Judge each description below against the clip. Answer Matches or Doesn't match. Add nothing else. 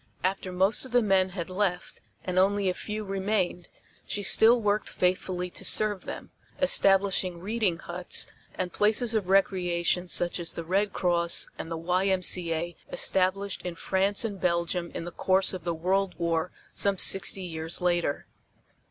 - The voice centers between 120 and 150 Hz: Doesn't match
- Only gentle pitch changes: Matches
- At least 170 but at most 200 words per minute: Doesn't match